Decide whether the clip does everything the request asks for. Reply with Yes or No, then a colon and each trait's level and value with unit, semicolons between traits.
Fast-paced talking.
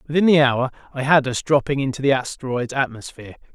No: average, 185 wpm